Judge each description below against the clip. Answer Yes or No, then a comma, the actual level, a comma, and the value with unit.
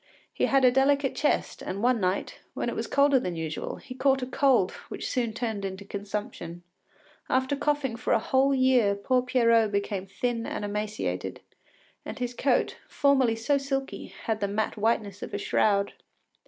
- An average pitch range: Yes, average, 4.6 semitones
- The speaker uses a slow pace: No, average, 175 wpm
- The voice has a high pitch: Yes, high, 230 Hz